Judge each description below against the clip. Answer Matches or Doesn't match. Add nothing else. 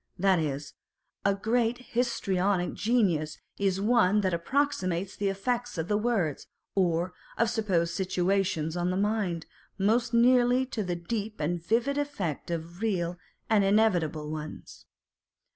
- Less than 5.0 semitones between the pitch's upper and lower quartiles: Matches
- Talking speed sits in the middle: Doesn't match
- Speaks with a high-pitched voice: Matches